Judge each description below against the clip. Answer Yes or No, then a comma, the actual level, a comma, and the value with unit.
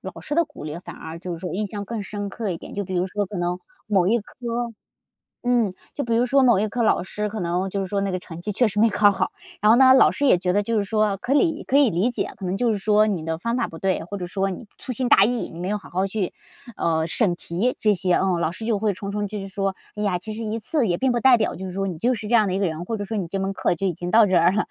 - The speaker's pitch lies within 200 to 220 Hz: Yes, high, 205 Hz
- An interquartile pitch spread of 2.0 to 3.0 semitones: No, average, 3.7 semitones